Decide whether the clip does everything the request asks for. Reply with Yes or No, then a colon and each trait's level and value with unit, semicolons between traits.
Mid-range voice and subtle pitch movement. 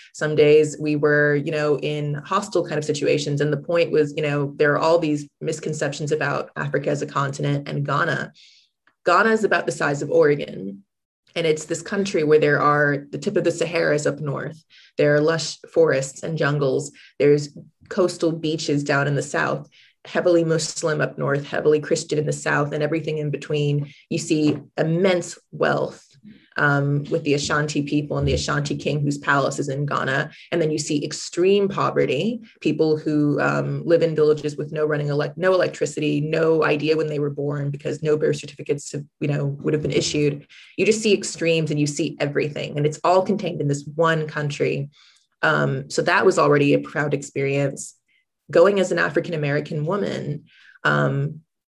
Yes: medium, 150 Hz; narrow, 2.1 semitones